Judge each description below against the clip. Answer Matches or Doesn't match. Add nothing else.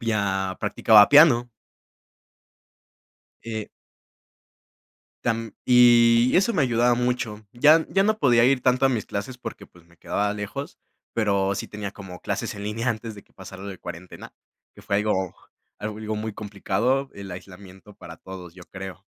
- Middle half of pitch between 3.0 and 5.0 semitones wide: Matches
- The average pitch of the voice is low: Matches